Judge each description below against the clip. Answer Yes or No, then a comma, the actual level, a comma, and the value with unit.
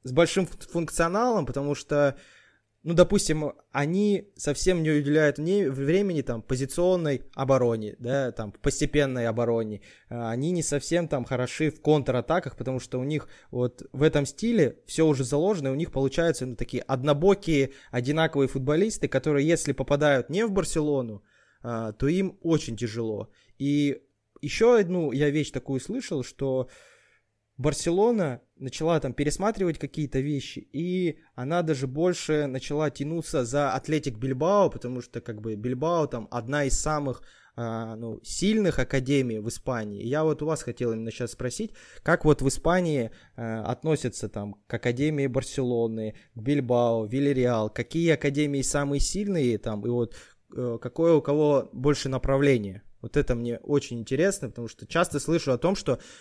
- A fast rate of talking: No, average, 150 wpm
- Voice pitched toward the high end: No, medium, 140 Hz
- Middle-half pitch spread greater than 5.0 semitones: No, average, 4.2 semitones